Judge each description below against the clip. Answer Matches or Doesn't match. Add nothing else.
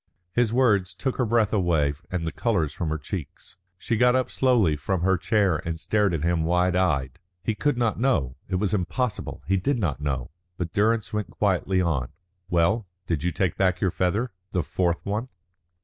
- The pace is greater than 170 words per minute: Matches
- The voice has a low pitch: Matches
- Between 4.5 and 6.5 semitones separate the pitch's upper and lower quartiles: Matches